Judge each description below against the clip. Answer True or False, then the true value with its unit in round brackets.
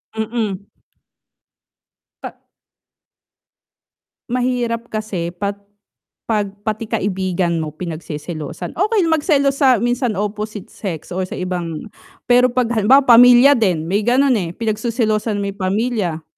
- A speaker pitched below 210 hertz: False (215 Hz)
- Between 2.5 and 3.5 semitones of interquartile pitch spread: False (4.8 semitones)